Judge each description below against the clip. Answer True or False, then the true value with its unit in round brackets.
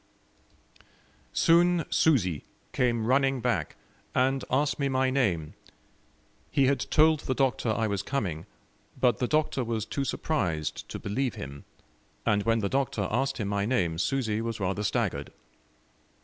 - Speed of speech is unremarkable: True (145 wpm)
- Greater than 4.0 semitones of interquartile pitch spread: True (5.0 semitones)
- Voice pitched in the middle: False (120 Hz)